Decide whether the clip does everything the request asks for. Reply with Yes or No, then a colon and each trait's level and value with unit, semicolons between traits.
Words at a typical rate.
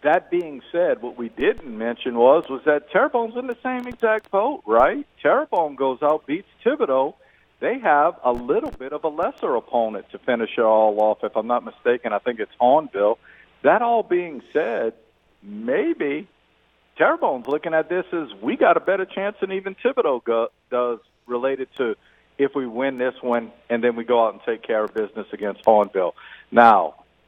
Yes: average, 185 wpm